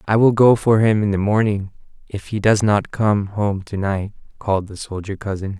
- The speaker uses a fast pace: Yes, fast, 215 wpm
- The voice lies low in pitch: Yes, low, 105 Hz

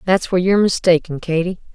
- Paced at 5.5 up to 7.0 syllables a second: Yes, 6.7 syllables/s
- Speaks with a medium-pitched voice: Yes, medium, 180 Hz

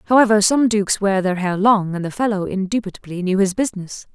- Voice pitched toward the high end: Yes, high, 200 Hz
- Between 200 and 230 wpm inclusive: Yes, fast, 205 wpm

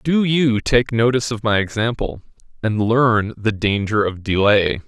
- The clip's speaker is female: No, male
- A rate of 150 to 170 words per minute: Yes, average, 160 wpm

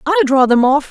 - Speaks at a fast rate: Yes, fast, 265 wpm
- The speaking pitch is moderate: No, very high, 285 Hz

